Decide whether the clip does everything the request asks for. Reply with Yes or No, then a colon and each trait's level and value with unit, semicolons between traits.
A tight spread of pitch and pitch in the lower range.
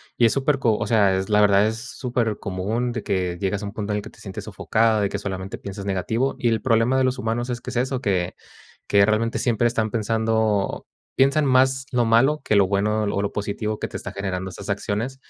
No: average, 3.2 semitones; low, 110 Hz